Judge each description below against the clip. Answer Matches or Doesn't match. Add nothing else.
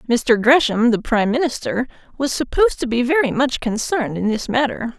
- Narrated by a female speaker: Matches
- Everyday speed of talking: Matches